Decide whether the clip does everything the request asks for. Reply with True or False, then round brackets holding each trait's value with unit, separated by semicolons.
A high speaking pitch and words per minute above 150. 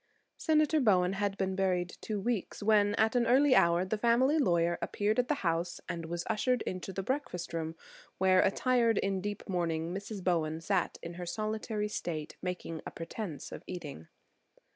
True (195 Hz; 170 wpm)